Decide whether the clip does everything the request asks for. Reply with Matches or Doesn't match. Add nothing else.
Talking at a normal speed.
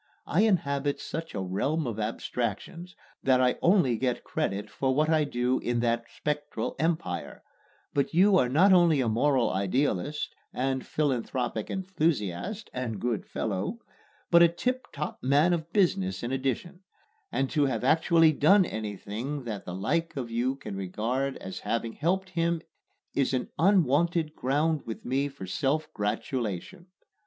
Matches